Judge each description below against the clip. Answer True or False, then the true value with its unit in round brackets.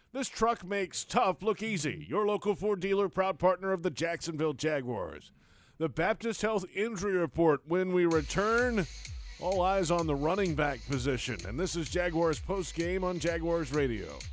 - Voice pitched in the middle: True (175 Hz)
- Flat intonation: False (4.2 semitones)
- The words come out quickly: False (165 wpm)